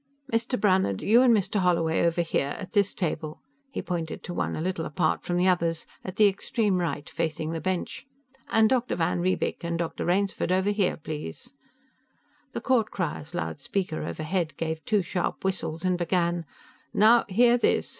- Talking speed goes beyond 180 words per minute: No, average, 175 wpm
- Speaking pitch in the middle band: Yes, medium, 180 Hz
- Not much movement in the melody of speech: No, average, 3.5 semitones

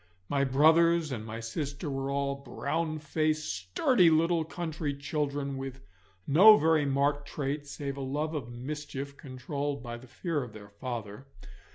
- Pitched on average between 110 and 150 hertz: Yes, medium, 140 Hz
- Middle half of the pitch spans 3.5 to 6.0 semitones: No, average, 2.7 semitones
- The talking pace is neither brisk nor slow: Yes, average, 150 wpm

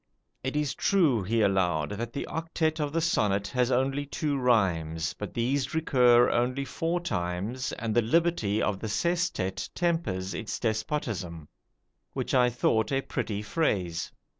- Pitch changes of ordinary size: No, wide, 6.4 semitones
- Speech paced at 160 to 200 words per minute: No, average, 150 wpm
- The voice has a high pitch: No, low, 120 Hz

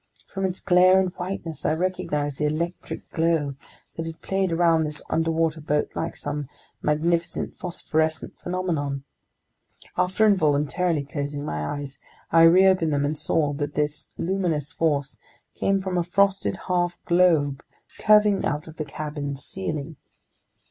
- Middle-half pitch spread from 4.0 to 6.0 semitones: No, average, 3.5 semitones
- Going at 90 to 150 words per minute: Yes, average, 140 wpm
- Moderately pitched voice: Yes, medium, 165 Hz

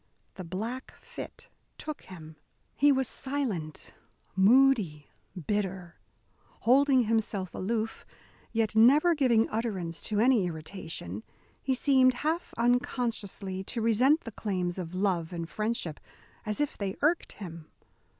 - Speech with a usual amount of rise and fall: No, wide, 5.7 semitones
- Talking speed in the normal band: No, slow, 120 wpm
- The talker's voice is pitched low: No, high, 215 Hz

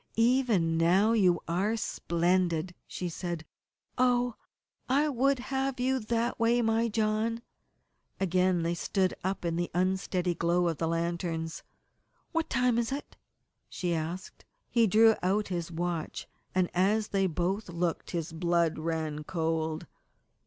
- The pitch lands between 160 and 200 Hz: Yes, medium, 185 Hz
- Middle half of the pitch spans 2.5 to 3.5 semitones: No, average, 5.1 semitones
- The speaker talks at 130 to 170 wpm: Yes, average, 140 wpm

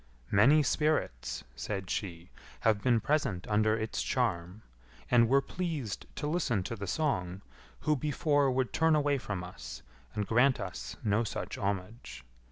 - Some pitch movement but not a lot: No, wide, 6.6 semitones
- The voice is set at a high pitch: No, low, 110 Hz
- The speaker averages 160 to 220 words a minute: No, average, 150 wpm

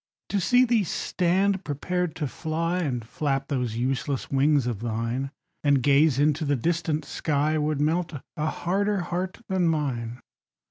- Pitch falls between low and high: Yes, medium, 150 Hz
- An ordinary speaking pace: Yes, average, 150 wpm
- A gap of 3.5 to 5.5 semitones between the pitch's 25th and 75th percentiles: Yes, average, 4.4 semitones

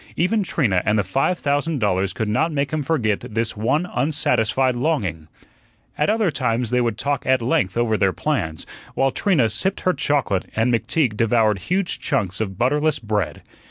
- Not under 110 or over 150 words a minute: No, average, 175 wpm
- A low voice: Yes, low, 125 Hz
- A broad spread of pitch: Yes, wide, 5.8 semitones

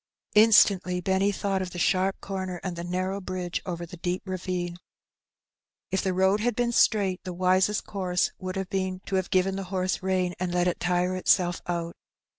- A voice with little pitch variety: Yes, narrow, 1.2 semitones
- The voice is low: No, medium, 185 Hz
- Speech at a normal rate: Yes, average, 190 wpm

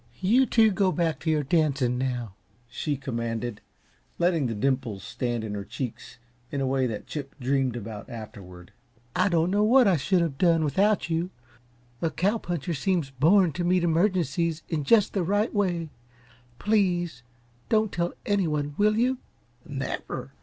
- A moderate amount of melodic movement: No, wide, 6.3 semitones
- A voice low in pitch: No, medium, 160 Hz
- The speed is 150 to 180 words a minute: Yes, average, 160 wpm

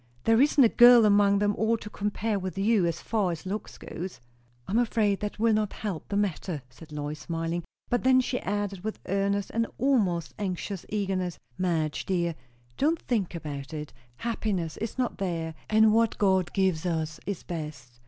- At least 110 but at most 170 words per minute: No, average, 185 wpm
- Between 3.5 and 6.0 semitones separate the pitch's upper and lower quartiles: Yes, average, 4.4 semitones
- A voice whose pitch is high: Yes, high, 195 Hz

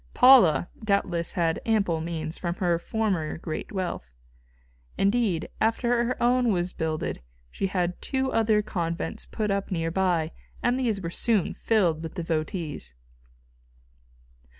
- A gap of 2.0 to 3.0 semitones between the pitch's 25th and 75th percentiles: No, average, 5.0 semitones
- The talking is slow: Yes, slow, 130 wpm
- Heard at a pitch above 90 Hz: Yes, medium, 185 Hz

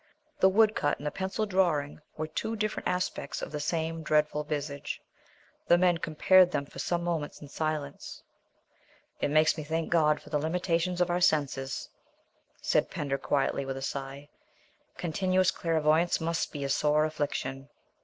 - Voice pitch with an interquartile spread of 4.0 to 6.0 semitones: No, average, 3.1 semitones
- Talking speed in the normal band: Yes, average, 160 wpm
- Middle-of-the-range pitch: Yes, medium, 155 Hz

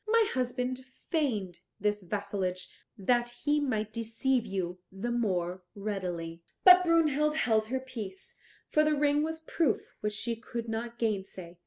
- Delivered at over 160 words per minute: No, average, 150 wpm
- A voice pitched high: Yes, high, 230 Hz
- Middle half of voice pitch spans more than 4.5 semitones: Yes, wide, 5.6 semitones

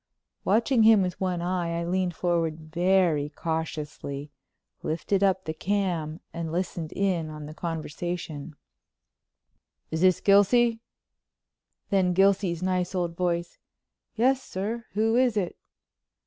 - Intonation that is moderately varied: Yes, average, 3.4 semitones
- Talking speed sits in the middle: No, slow, 120 wpm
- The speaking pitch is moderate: Yes, medium, 180 Hz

